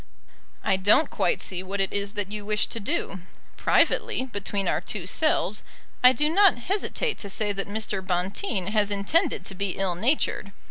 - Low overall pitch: No, high, 205 Hz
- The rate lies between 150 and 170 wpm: No, average, 180 wpm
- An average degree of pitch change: Yes, average, 3.7 semitones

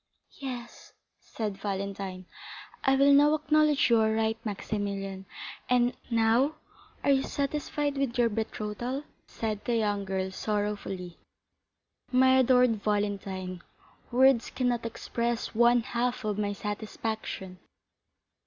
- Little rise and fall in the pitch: No, average, 3.9 semitones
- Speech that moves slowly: Yes, slow, 115 wpm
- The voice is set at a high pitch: Yes, high, 225 Hz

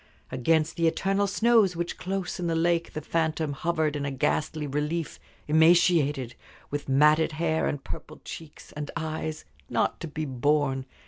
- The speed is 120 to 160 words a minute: Yes, average, 155 wpm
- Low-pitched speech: No, medium, 155 Hz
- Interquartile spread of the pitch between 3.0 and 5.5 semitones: No, narrow, 2.4 semitones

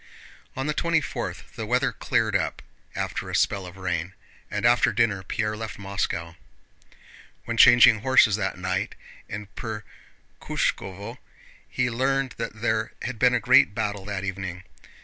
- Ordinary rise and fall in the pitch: Yes, average, 3.7 semitones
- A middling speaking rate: Yes, average, 150 wpm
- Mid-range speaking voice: No, low, 105 Hz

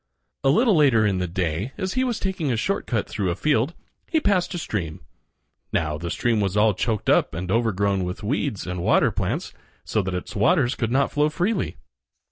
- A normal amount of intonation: No, wide, 8.3 semitones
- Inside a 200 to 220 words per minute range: Yes, fast, 205 wpm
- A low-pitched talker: Yes, low, 110 Hz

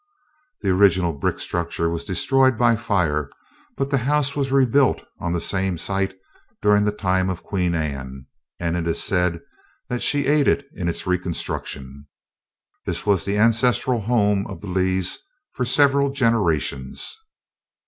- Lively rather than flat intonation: Yes, wide, 6.2 semitones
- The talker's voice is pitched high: No, very low, 95 Hz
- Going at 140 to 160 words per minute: Yes, average, 150 wpm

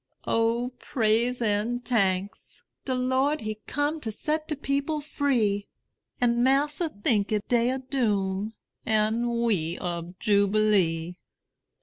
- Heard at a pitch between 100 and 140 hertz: No, high, 230 Hz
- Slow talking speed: Yes, slow, 120 wpm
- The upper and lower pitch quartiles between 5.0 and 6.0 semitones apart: No, average, 4.3 semitones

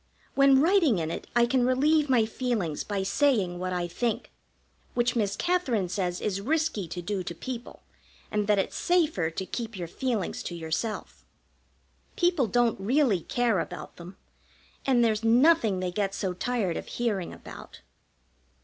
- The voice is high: Yes, high, 220 Hz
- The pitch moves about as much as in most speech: No, wide, 5.7 semitones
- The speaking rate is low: No, average, 160 wpm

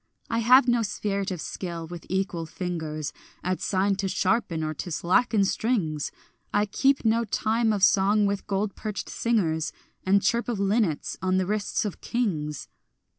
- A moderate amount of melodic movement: Yes, average, 3.8 semitones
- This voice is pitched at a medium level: No, high, 195 Hz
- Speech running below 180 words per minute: Yes, average, 165 wpm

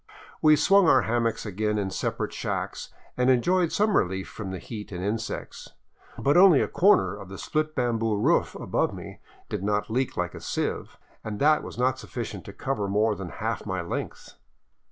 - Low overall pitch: Yes, low, 115 Hz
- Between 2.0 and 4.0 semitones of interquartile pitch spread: No, average, 5.1 semitones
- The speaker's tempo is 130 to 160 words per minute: No, average, 180 wpm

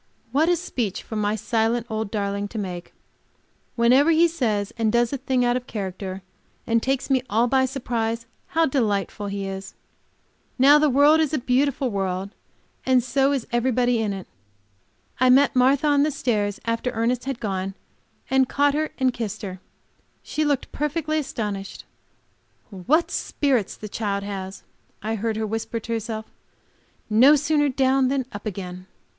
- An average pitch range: Yes, average, 4.7 semitones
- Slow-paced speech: No, average, 165 wpm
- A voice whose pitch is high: Yes, high, 235 Hz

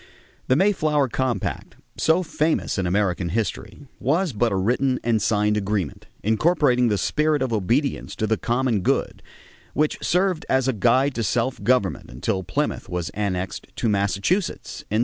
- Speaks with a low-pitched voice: Yes, low, 115 Hz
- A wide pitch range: Yes, wide, 5.7 semitones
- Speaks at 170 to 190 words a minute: No, average, 160 wpm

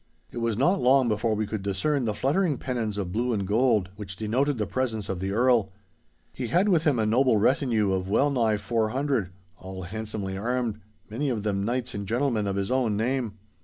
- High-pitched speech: No, low, 110 Hz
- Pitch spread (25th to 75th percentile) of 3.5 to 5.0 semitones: Yes, average, 4.0 semitones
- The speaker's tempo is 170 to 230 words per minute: Yes, average, 200 wpm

